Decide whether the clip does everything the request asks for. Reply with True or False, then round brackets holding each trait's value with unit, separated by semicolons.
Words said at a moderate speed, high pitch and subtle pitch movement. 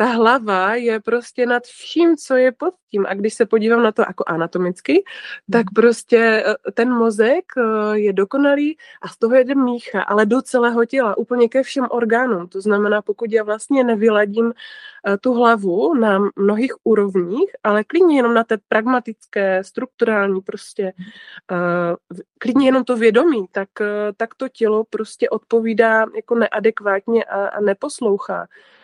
False (150 wpm; 225 Hz; 3.0 semitones)